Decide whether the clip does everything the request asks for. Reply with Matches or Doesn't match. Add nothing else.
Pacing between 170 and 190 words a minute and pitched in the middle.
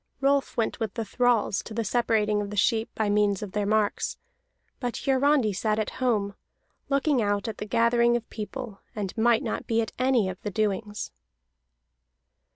Doesn't match